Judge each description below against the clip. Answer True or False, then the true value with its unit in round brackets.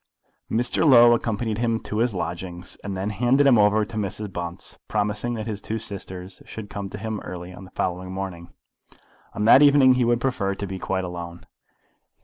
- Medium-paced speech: True (190 wpm)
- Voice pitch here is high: False (105 Hz)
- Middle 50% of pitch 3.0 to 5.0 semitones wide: True (3.8 semitones)